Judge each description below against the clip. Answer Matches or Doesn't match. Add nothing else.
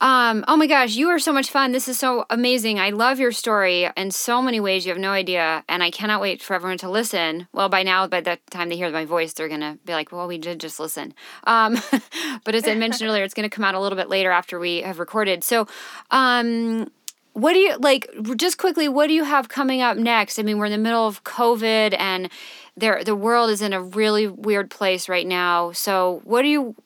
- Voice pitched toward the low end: Doesn't match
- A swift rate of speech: Matches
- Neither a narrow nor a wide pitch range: Matches